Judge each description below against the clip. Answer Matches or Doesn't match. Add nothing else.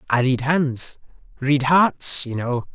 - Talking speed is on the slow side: Matches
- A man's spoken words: Matches